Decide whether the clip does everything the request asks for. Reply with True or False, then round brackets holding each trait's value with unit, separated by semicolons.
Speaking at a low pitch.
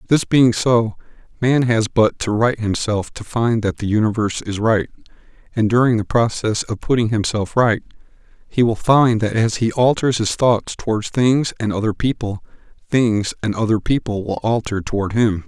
True (115 Hz)